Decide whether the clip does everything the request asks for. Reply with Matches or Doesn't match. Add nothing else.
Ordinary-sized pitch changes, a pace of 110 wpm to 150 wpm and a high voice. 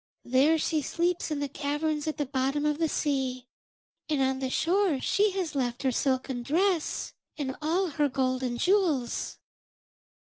Doesn't match